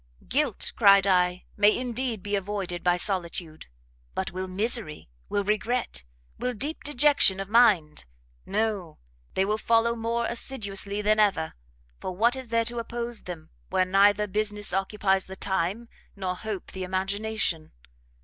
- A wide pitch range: No, average, 3.5 semitones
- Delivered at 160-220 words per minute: No, average, 145 wpm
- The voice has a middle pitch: No, high, 205 Hz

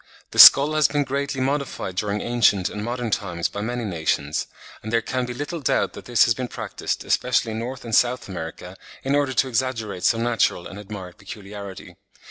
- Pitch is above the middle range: No, low, 115 Hz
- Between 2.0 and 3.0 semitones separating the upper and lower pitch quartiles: No, average, 4.4 semitones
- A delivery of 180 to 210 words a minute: Yes, average, 195 wpm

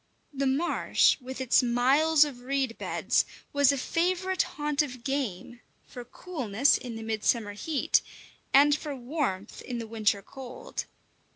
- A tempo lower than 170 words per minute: Yes, average, 145 wpm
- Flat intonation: No, average, 3.7 semitones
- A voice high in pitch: Yes, very high, 265 Hz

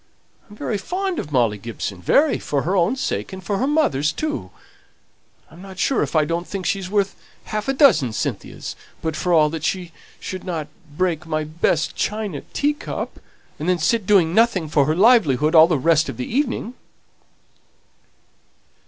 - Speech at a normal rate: Yes, average, 170 wpm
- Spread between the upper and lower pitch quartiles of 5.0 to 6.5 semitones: Yes, wide, 5.5 semitones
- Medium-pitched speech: Yes, medium, 180 Hz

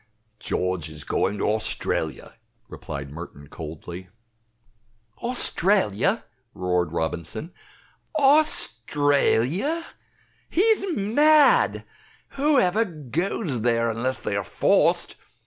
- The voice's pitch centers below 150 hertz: Yes, medium, 140 Hz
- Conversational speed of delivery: No, slow, 85 wpm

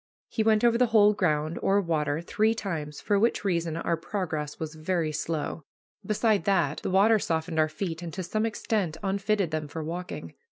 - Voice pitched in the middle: Yes, medium, 175 Hz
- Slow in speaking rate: No, average, 190 wpm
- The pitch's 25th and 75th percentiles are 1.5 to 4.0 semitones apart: No, average, 4.6 semitones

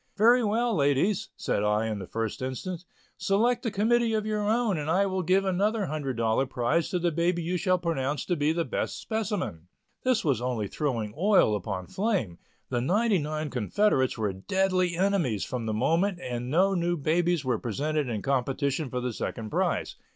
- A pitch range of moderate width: No, wide, 7.8 semitones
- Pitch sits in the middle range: Yes, medium, 160 Hz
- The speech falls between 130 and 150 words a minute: No, average, 185 wpm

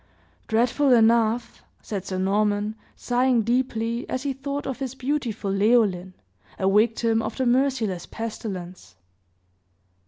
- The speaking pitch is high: Yes, high, 230 Hz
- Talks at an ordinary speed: No, slow, 120 wpm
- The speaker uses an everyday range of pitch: Yes, average, 3.5 semitones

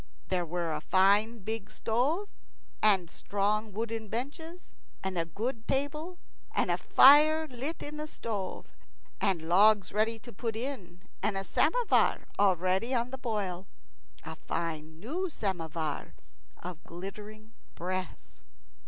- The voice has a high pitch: Yes, high, 215 Hz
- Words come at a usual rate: No, slow, 130 wpm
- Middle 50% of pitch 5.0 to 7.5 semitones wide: Yes, average, 5.3 semitones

